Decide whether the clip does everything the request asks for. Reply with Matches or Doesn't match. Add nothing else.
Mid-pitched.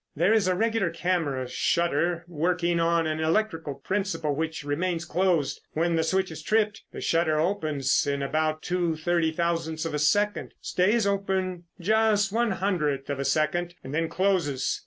Matches